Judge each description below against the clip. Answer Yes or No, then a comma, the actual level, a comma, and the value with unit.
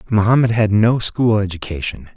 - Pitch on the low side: Yes, low, 105 Hz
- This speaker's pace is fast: No, average, 140 wpm